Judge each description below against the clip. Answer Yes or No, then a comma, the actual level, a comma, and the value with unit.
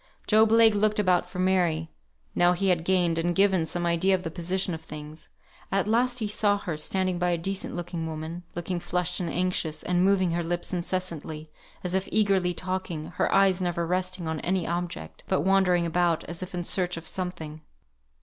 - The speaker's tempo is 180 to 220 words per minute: Yes, average, 195 wpm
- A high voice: No, medium, 180 Hz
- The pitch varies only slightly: Yes, narrow, 2.0 semitones